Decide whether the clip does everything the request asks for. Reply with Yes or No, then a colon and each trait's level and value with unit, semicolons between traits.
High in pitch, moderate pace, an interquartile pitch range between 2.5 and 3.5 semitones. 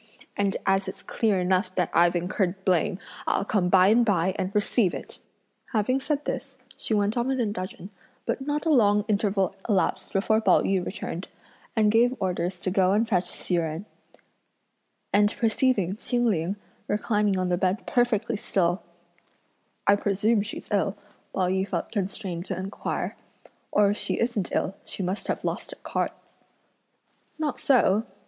Yes: high, 200 Hz; average, 165 wpm; average, 3.1 semitones